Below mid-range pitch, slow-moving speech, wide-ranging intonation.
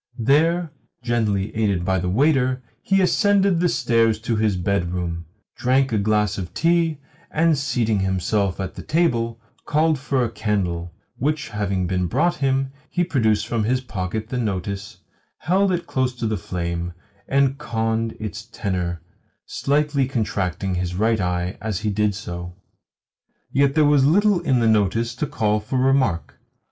No: low, 115 Hz; average, 155 wpm; wide, 6.1 semitones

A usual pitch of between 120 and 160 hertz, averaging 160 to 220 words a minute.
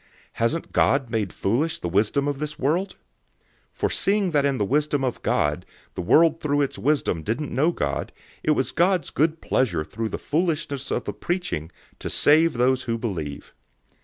Yes: medium, 140 Hz; average, 180 wpm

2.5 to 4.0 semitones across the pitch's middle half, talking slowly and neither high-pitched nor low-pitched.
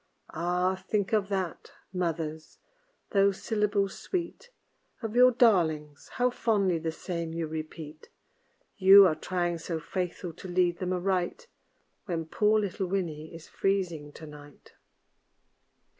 Yes: average, 3.5 semitones; slow, 130 wpm; medium, 180 Hz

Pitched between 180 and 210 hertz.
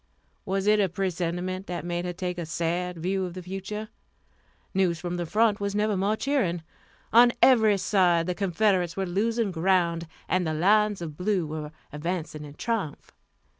Yes: medium, 185 Hz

